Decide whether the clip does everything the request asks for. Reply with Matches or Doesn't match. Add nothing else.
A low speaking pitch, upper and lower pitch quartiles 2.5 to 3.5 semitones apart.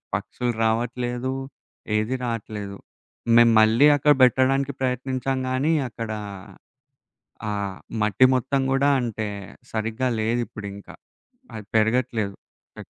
Matches